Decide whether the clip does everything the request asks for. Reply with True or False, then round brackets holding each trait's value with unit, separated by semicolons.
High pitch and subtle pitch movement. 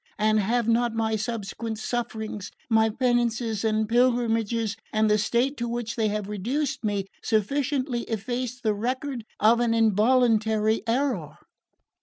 True (225 Hz; 2.0 semitones)